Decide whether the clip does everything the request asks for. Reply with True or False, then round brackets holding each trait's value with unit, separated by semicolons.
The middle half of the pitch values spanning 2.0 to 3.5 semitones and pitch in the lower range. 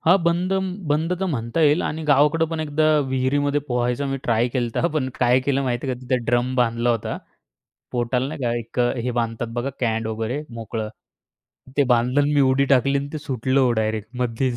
True (3.2 semitones; 130 Hz)